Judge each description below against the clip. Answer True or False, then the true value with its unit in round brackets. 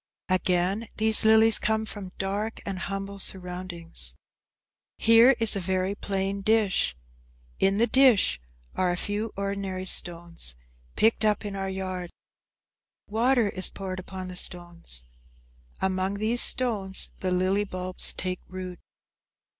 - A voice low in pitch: False (195 Hz)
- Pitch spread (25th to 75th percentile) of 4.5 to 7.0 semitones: False (2.6 semitones)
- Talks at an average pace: False (130 wpm)